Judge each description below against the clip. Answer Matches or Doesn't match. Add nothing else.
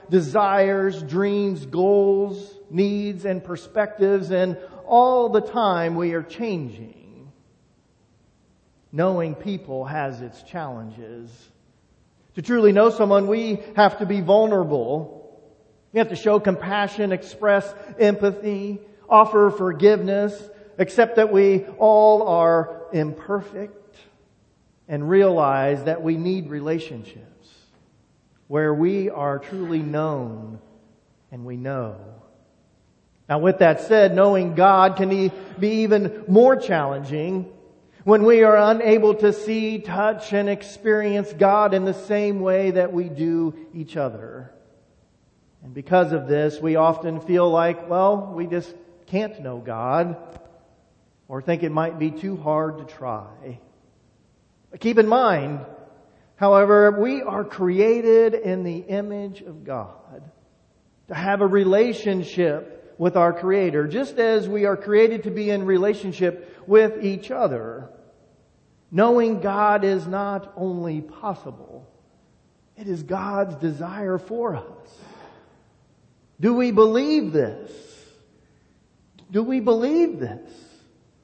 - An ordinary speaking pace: Doesn't match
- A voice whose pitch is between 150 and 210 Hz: Matches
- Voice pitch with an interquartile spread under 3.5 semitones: Doesn't match